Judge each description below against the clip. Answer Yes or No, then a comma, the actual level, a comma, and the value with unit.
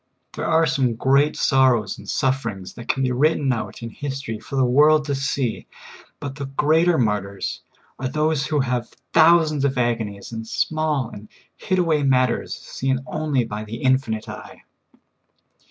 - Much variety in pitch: No, average, 4.2 semitones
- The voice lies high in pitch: No, low, 130 Hz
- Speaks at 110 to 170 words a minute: Yes, average, 160 wpm